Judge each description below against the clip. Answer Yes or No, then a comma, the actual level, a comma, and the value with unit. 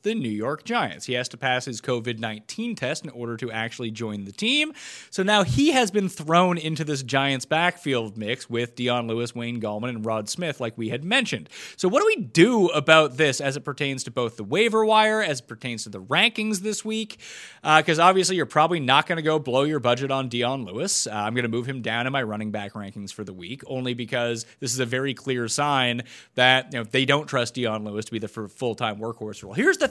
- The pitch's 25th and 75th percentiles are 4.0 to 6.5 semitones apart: Yes, wide, 5.4 semitones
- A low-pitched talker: Yes, low, 130 Hz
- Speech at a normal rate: No, fast, 245 wpm